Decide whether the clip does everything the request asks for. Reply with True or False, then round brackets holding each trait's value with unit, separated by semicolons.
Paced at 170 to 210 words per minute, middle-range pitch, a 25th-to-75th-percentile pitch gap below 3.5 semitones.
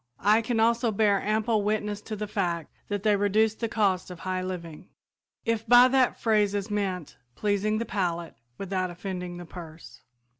False (175 wpm; 205 Hz; 2.9 semitones)